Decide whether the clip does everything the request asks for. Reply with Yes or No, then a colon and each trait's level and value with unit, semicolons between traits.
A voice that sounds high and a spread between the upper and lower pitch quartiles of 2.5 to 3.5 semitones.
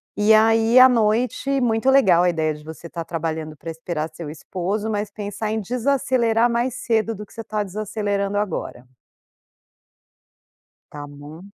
No: high, 210 Hz; average, 5.3 semitones